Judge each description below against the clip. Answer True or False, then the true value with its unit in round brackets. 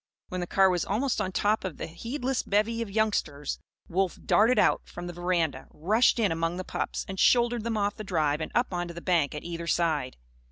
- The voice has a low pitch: False (185 Hz)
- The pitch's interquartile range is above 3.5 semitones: True (4.4 semitones)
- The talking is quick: True (215 wpm)